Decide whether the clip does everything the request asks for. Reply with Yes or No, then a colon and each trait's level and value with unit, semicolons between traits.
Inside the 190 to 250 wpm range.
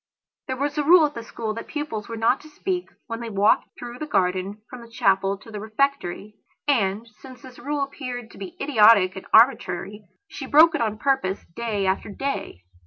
Yes: fast, 205 wpm